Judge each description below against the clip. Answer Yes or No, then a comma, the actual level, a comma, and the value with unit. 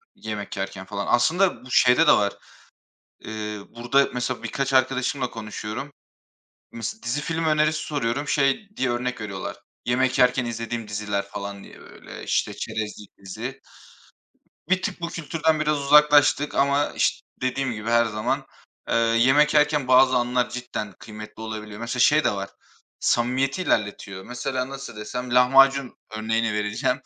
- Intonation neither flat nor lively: Yes, average, 4.2 semitones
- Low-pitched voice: Yes, low, 125 Hz